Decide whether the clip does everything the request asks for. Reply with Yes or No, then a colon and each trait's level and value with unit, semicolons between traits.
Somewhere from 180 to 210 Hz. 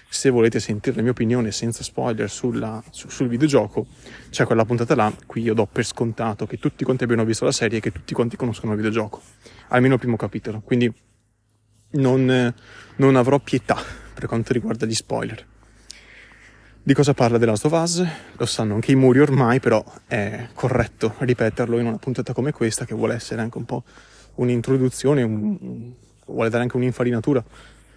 No: low, 115 Hz